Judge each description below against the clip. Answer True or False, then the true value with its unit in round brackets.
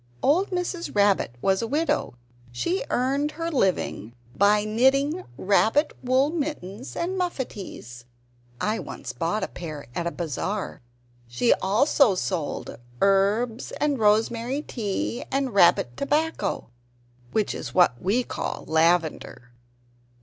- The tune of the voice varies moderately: False (7.7 semitones)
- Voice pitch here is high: True (215 Hz)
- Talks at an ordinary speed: False (120 wpm)